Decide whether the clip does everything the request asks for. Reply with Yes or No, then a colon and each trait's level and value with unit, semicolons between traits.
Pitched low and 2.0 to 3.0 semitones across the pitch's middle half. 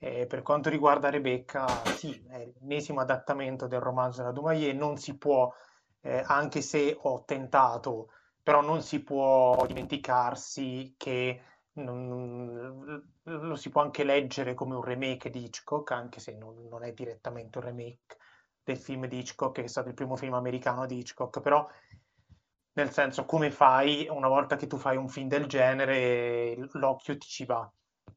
Yes: low, 130 Hz; narrow, 2.5 semitones